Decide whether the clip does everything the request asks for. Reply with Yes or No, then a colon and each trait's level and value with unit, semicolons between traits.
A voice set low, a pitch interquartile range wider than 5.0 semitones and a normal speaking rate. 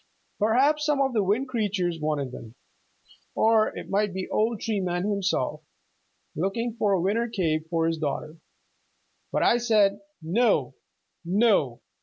No: high, 200 Hz; wide, 5.5 semitones; average, 145 wpm